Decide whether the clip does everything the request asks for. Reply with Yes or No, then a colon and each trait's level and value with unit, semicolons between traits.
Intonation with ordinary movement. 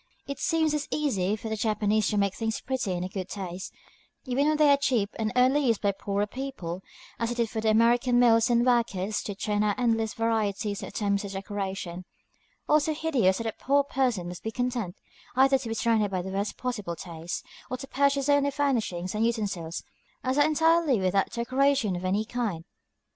Yes: average, 4.8 semitones